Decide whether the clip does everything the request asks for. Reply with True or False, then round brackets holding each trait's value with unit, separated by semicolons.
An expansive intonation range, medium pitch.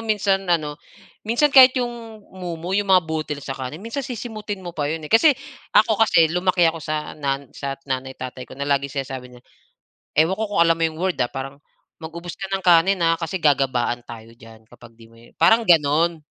True (5.7 semitones; 165 Hz)